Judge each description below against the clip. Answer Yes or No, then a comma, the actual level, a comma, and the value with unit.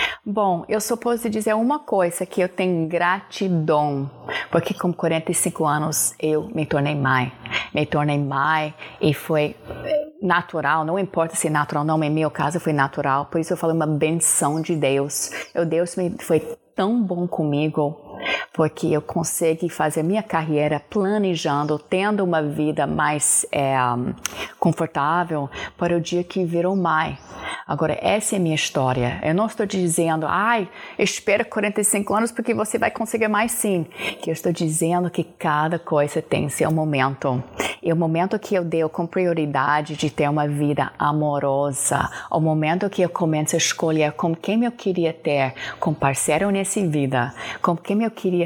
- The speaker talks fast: No, average, 165 wpm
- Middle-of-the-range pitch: Yes, medium, 165 Hz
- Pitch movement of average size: Yes, average, 3.8 semitones